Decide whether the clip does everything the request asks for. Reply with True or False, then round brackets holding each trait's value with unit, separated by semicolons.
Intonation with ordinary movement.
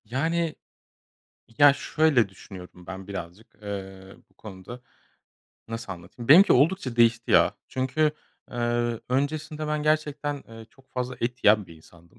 False (6.7 semitones)